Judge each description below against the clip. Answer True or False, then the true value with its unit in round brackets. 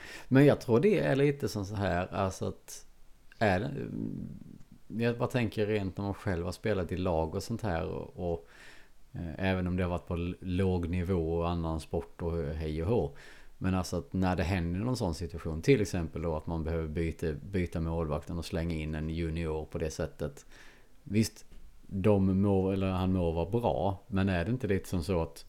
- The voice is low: True (90 Hz)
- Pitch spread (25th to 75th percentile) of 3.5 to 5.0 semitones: False (3.0 semitones)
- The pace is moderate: False (205 wpm)